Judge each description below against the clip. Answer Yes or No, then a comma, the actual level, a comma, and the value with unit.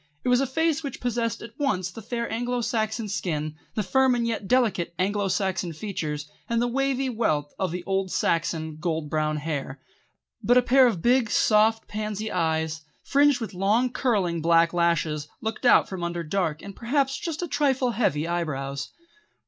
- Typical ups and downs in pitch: No, wide, 6.5 semitones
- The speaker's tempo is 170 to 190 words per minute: Yes, average, 180 wpm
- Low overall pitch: No, high, 205 Hz